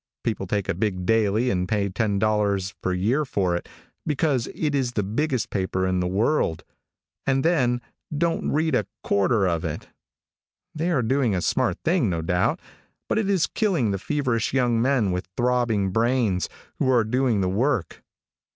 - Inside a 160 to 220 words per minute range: Yes, average, 170 wpm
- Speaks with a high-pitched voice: No, low, 115 Hz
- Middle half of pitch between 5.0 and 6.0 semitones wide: Yes, wide, 5.5 semitones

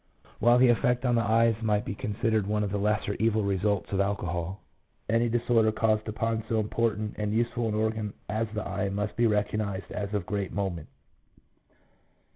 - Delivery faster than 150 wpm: Yes, average, 180 wpm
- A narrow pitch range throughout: Yes, narrow, 1.9 semitones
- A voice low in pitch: Yes, low, 105 Hz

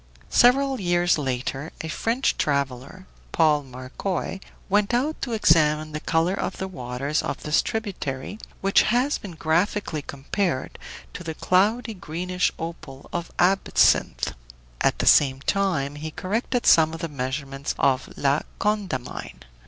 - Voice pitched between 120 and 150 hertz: No, medium, 165 Hz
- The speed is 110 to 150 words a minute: Yes, slow, 135 wpm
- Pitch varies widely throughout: Yes, wide, 5.9 semitones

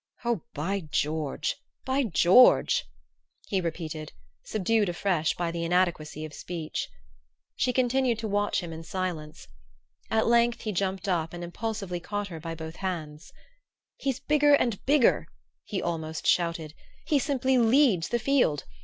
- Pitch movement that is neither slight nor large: No, wide, 6.3 semitones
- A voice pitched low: No, medium, 185 Hz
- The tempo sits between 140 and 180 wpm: Yes, average, 145 wpm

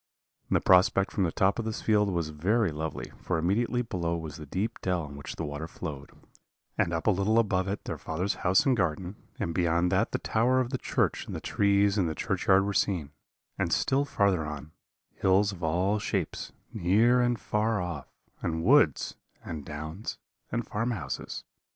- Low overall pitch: Yes, very low, 95 Hz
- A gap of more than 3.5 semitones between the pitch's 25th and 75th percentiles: Yes, average, 4.7 semitones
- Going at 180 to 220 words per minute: Yes, average, 190 wpm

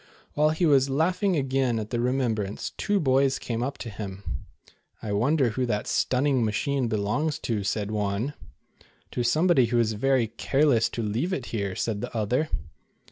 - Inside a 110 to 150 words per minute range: No, average, 180 wpm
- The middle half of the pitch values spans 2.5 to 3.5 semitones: No, average, 4.4 semitones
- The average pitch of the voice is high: No, low, 125 Hz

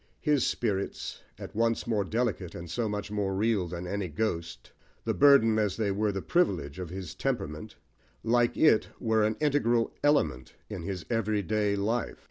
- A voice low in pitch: Yes, low, 105 Hz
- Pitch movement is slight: No, average, 3.3 semitones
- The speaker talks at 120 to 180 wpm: Yes, average, 165 wpm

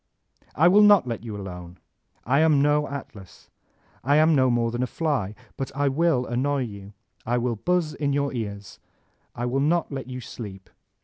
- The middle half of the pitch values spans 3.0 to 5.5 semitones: Yes, average, 4.4 semitones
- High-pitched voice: No, low, 130 Hz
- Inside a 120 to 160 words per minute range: No, average, 190 wpm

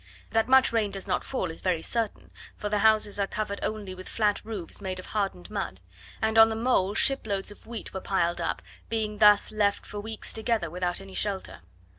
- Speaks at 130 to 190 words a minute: No, fast, 205 wpm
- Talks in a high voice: Yes, high, 205 Hz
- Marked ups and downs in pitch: No, narrow, 2.5 semitones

